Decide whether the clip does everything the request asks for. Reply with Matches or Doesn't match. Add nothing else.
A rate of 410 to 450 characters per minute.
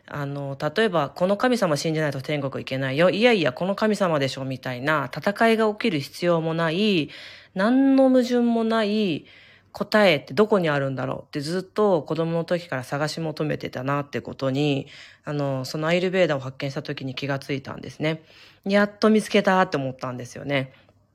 Doesn't match